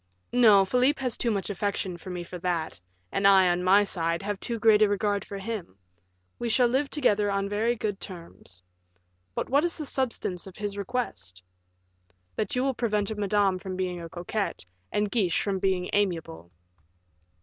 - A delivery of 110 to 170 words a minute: No, average, 180 wpm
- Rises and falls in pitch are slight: No, average, 3.5 semitones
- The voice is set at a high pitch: Yes, high, 200 Hz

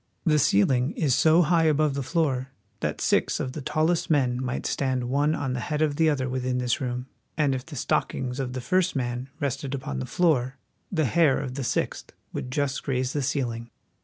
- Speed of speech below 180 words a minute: No, fast, 205 wpm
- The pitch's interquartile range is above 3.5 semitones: No, average, 3.2 semitones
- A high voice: No, low, 135 Hz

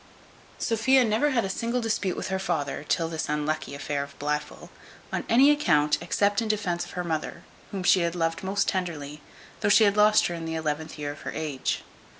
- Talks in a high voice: No, medium, 175 Hz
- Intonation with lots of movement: Yes, wide, 5.7 semitones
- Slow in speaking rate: No, average, 200 wpm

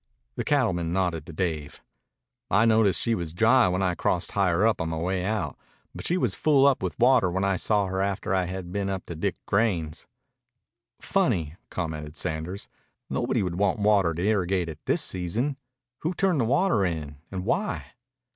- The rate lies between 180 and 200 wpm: Yes, average, 185 wpm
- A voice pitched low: Yes, very low, 95 Hz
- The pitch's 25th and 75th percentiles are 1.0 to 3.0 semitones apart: No, average, 4.3 semitones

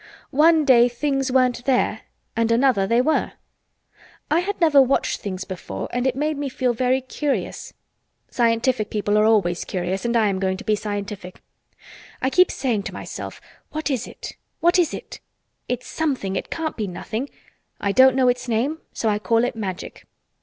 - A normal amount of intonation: Yes, average, 4.5 semitones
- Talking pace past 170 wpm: Yes, average, 180 wpm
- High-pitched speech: Yes, high, 245 Hz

